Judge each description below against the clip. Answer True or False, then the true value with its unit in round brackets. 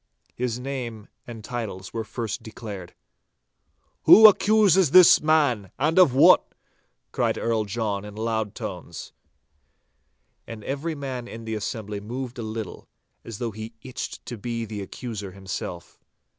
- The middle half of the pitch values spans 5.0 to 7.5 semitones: False (3.7 semitones)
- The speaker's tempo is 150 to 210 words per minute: False (140 wpm)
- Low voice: True (115 Hz)